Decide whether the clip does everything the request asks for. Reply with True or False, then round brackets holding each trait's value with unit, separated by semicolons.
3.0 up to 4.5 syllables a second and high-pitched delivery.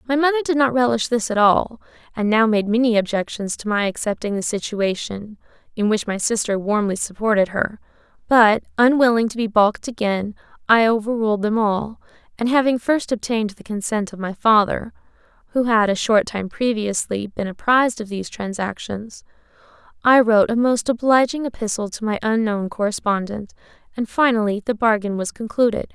False (4.8 syllables/s; 220 Hz)